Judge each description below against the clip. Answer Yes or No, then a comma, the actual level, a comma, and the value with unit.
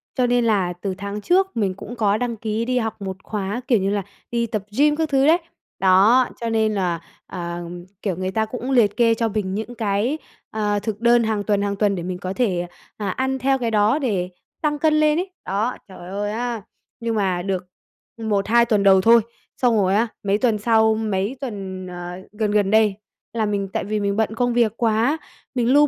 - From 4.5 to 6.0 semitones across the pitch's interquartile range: No, average, 3.3 semitones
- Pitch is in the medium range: No, high, 215 Hz